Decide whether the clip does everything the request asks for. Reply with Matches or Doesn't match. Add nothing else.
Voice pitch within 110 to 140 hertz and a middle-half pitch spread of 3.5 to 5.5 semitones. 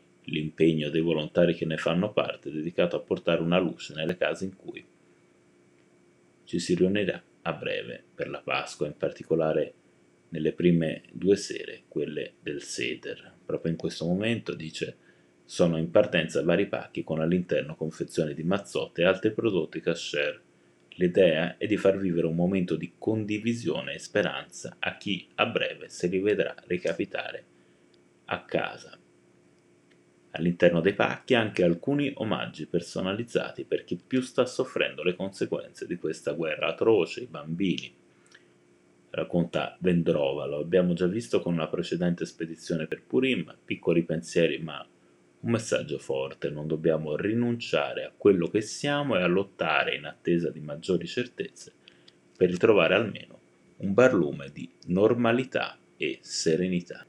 Doesn't match